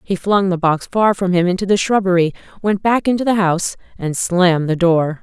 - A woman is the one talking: Yes, female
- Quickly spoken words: Yes, fast, 220 wpm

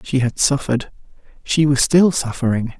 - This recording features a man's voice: Yes, male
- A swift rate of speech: No, average, 150 wpm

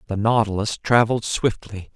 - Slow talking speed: Yes, slow, 125 wpm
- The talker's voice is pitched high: No, low, 110 Hz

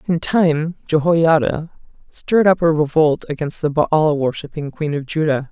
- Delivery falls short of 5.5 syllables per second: Yes, 4.5 syllables/s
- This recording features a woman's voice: Yes, female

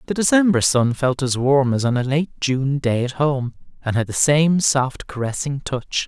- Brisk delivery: Yes, fast, 210 wpm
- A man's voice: Yes, male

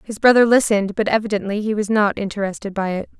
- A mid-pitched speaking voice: No, high, 210 Hz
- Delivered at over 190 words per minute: Yes, fast, 205 wpm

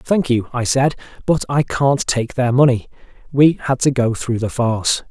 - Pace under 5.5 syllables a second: Yes, 4.5 syllables/s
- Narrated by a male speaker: Yes, male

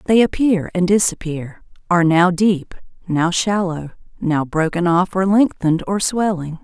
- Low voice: No, medium, 180 Hz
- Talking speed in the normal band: Yes, average, 145 wpm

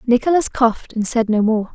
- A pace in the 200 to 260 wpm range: Yes, fast, 205 wpm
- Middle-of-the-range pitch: No, high, 235 Hz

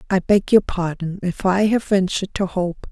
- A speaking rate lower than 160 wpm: No, fast, 205 wpm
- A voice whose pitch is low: No, high, 190 Hz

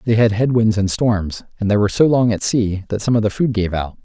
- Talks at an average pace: No, fast, 295 wpm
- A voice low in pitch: Yes, low, 105 Hz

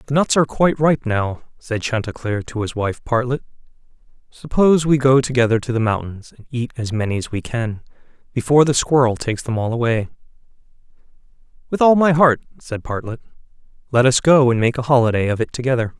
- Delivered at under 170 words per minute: No, average, 185 wpm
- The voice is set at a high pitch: No, low, 125 Hz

